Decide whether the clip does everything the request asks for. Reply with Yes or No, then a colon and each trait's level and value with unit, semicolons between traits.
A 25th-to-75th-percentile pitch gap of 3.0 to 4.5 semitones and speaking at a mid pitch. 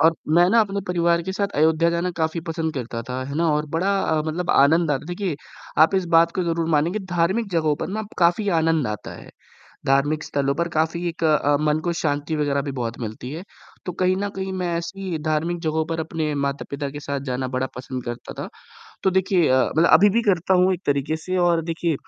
Yes: average, 3.3 semitones; medium, 165 Hz